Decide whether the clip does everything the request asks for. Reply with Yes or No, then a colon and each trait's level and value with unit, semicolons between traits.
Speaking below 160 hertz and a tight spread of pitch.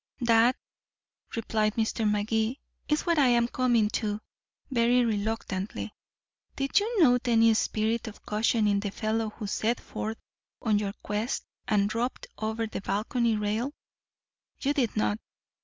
No: high, 225 Hz; narrow, 2.2 semitones